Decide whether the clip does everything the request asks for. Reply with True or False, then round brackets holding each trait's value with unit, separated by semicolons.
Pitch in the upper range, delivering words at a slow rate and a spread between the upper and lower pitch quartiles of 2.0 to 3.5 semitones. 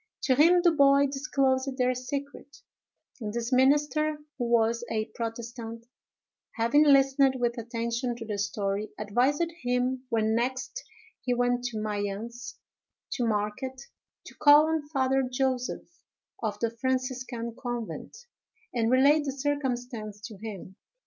True (250 Hz; 130 wpm; 3.0 semitones)